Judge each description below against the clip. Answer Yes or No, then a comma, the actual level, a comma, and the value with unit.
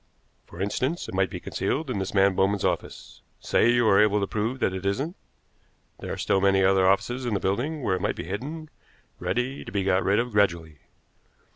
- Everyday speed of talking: No, fast, 215 wpm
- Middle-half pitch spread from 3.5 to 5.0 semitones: Yes, average, 4.3 semitones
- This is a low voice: Yes, low, 100 Hz